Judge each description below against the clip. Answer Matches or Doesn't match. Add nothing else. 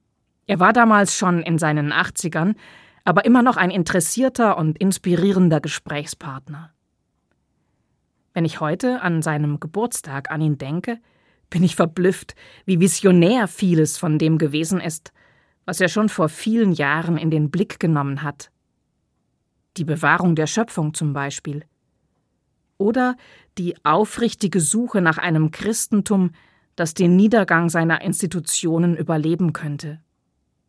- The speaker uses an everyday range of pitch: Matches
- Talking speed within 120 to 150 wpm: Matches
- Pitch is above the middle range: Doesn't match